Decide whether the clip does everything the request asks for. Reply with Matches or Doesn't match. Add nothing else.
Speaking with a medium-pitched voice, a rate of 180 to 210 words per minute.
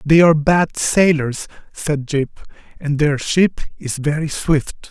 Doesn't match